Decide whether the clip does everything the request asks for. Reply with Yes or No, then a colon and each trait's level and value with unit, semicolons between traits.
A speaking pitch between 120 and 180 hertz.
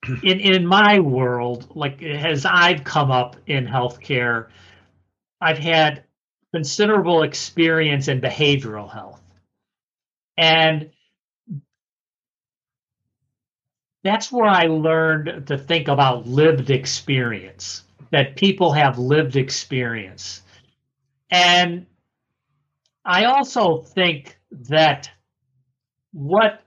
Yes: medium, 140 Hz